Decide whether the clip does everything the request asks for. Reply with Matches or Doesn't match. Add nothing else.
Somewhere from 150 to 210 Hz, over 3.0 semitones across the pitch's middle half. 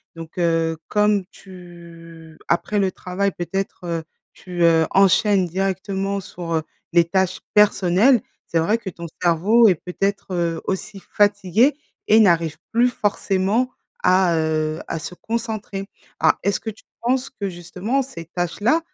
Matches